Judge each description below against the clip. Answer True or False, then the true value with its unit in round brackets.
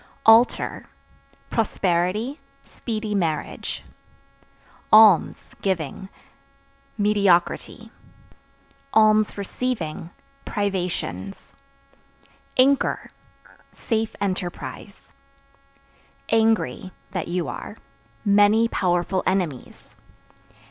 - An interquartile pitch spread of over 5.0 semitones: False (3.8 semitones)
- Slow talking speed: True (55 wpm)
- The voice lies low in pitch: False (200 Hz)